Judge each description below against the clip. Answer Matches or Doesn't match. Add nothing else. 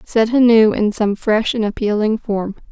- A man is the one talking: Doesn't match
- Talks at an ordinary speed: Matches